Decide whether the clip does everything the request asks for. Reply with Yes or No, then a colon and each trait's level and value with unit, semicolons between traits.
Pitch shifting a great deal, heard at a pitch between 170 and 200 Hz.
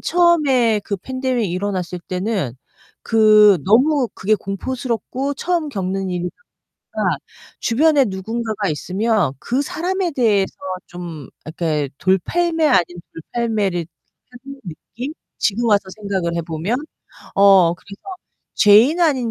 No: wide, 5.9 semitones; high, 215 Hz